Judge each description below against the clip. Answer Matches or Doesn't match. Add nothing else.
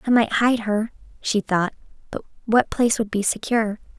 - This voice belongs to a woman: Matches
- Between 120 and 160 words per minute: Doesn't match